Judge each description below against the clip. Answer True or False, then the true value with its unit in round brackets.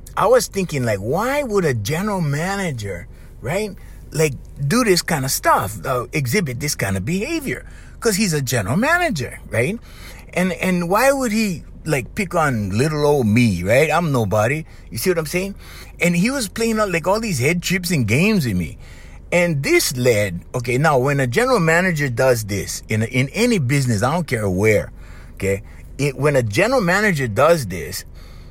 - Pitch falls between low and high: True (145 Hz)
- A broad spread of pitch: True (7.9 semitones)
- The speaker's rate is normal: True (185 wpm)